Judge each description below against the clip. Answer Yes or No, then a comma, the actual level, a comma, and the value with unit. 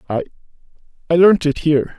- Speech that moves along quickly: No, average, 150 wpm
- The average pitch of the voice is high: No, medium, 155 Hz